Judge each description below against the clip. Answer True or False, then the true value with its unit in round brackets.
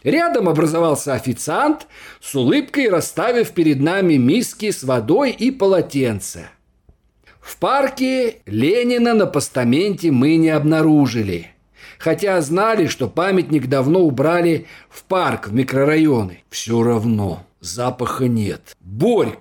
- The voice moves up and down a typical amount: False (7.8 semitones)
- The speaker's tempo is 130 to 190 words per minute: False (110 wpm)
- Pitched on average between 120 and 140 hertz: False (155 Hz)